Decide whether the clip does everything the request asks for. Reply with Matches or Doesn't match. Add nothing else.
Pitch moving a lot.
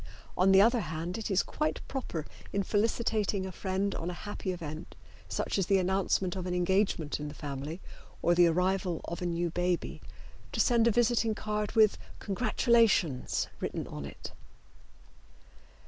Doesn't match